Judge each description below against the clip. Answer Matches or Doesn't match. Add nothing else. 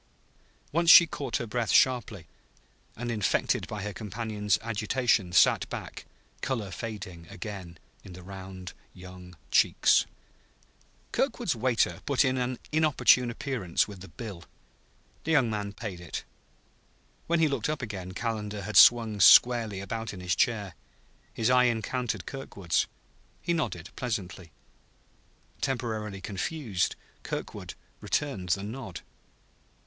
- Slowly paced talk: Matches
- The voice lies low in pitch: Matches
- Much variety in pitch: Doesn't match